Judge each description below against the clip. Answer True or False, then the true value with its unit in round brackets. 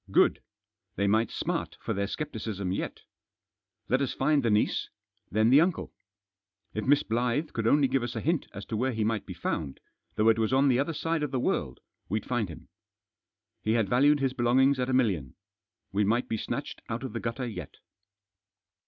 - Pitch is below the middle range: True (120 Hz)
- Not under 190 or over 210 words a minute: True (200 wpm)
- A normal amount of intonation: True (3.8 semitones)